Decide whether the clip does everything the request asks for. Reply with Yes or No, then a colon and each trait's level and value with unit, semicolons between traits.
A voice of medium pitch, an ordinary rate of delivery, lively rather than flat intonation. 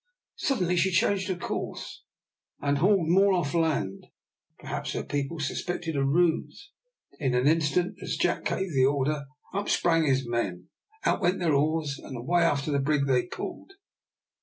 No: medium, 155 Hz; average, 165 wpm; average, 4.2 semitones